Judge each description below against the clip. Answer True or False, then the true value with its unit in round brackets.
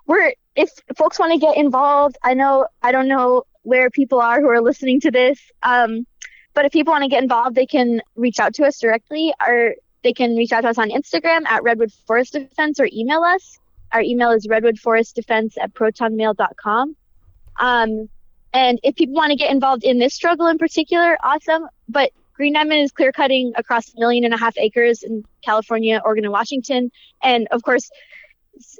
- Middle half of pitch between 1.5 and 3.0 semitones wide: False (3.8 semitones)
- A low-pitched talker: False (255 Hz)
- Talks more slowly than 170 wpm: False (195 wpm)